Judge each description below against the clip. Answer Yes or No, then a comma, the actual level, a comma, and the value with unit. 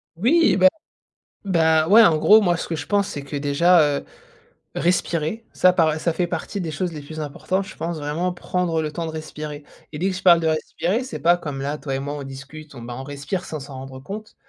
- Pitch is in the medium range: Yes, medium, 160 Hz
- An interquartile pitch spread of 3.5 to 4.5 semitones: Yes, average, 3.8 semitones